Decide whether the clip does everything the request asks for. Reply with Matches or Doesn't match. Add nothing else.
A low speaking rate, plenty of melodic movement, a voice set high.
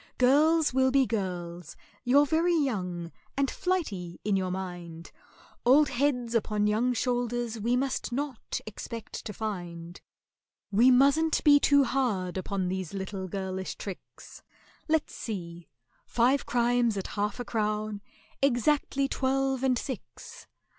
Matches